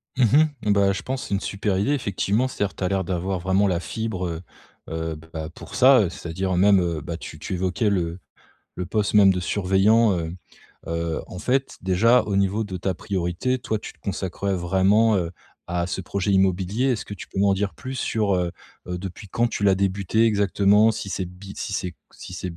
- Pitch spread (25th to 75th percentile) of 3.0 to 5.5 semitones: No, narrow, 2.6 semitones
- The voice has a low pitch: Yes, very low, 95 Hz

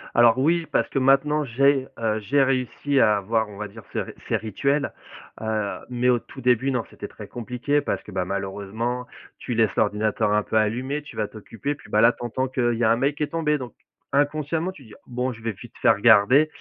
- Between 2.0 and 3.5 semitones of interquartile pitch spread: No, average, 4.2 semitones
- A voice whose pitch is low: Yes, low, 120 Hz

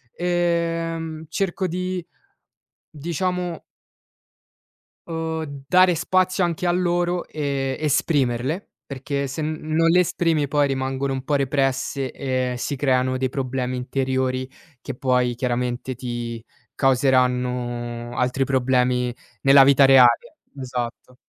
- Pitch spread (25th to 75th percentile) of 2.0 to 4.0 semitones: No, average, 4.5 semitones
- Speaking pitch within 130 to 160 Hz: Yes, low, 135 Hz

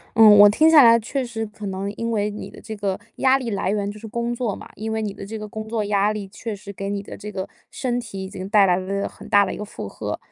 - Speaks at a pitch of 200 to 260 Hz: Yes, high, 210 Hz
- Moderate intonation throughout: No, narrow, 2.2 semitones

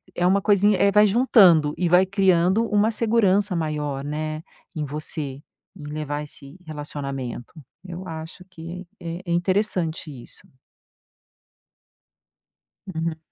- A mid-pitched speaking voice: Yes, medium, 170 Hz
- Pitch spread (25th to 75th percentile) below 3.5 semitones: No, average, 4.2 semitones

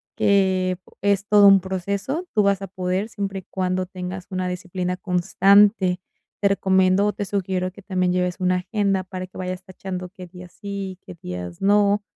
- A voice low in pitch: No, high, 190 Hz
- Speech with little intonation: Yes, narrow, 1.6 semitones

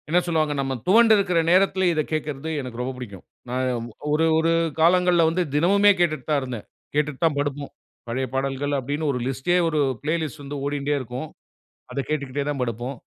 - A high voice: No, medium, 145 Hz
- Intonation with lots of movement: No, average, 3.6 semitones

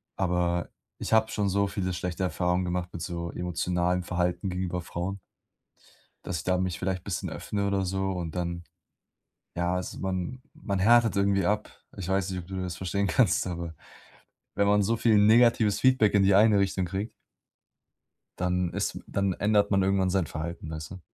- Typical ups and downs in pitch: No, narrow, 2.2 semitones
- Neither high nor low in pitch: No, very low, 95 Hz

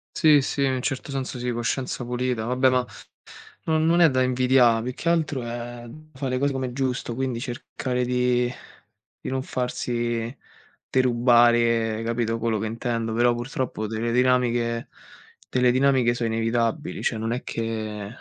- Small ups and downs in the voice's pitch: Yes, narrow, 1.8 semitones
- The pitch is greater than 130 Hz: No, low, 125 Hz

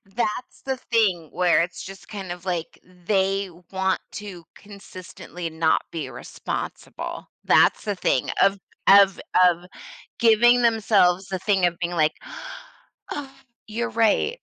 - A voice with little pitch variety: No, average, 3.6 semitones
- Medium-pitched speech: No, high, 195 Hz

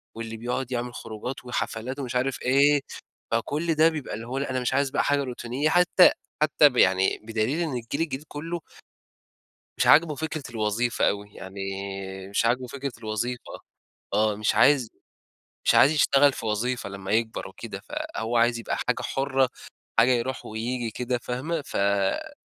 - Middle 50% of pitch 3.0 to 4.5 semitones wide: Yes, average, 3.8 semitones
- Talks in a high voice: No, low, 125 Hz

